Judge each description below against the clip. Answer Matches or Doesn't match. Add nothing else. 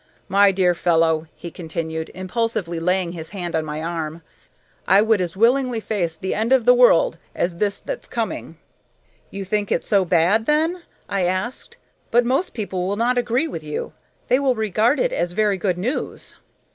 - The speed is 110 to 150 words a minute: Doesn't match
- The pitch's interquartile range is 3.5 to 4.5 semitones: Doesn't match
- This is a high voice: Matches